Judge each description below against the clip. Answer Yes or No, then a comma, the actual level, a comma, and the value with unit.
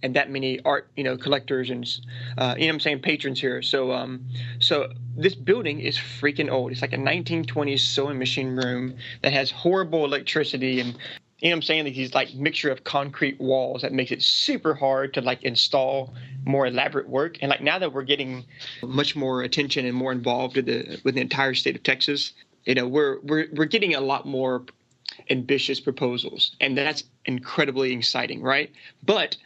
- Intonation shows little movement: Yes, narrow, 2.1 semitones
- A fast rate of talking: No, average, 195 wpm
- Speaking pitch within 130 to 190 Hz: Yes, low, 135 Hz